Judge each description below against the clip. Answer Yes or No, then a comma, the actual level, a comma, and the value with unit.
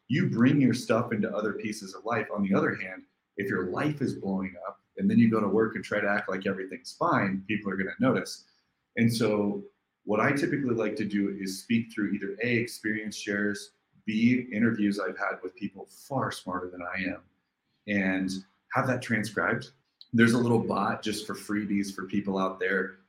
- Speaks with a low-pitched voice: Yes, low, 100 Hz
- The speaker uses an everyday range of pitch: No, narrow, 2.3 semitones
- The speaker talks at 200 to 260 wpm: Yes, fast, 205 wpm